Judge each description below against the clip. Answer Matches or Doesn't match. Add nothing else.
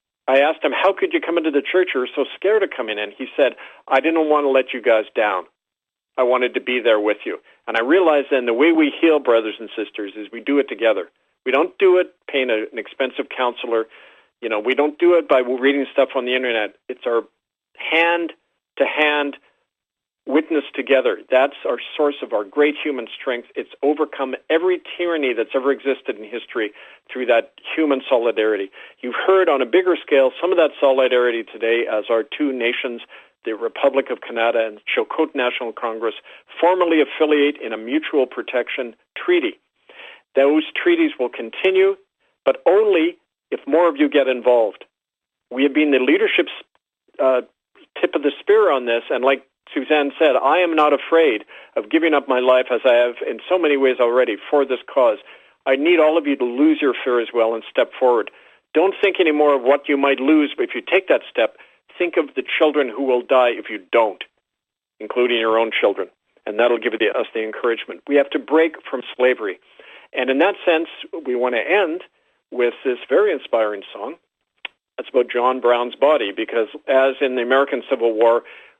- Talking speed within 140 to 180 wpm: Doesn't match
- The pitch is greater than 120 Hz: Matches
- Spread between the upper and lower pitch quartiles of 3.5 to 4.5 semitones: Doesn't match